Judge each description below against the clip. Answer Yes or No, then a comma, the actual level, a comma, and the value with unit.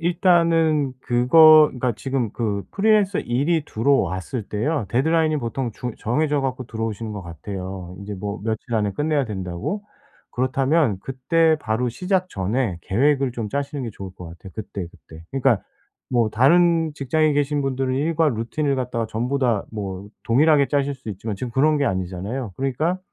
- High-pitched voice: No, low, 130 Hz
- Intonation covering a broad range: Yes, wide, 5.7 semitones